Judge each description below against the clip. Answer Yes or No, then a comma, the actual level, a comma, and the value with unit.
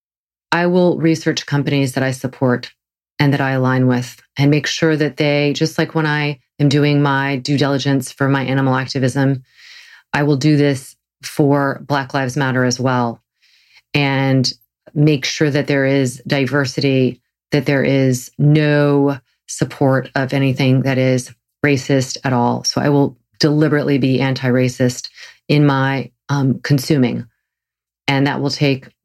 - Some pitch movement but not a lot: No, narrow, 2.0 semitones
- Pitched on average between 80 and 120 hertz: No, low, 135 Hz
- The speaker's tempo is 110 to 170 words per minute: Yes, average, 155 wpm